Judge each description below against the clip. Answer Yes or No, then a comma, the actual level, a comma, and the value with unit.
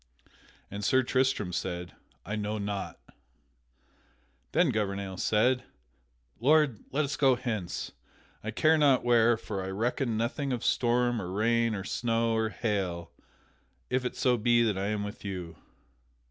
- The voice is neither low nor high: No, low, 115 Hz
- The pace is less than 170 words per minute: Yes, average, 145 wpm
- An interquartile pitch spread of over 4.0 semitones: No, average, 3.7 semitones